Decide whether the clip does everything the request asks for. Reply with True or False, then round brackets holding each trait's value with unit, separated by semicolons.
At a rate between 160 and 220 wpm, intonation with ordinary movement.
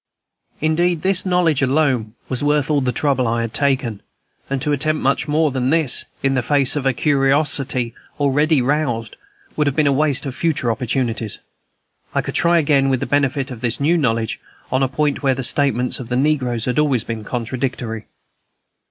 True (185 wpm; 3.2 semitones)